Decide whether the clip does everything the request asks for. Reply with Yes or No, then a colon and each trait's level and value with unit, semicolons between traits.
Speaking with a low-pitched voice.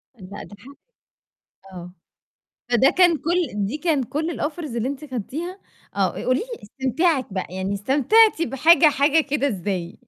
No: very high, 275 Hz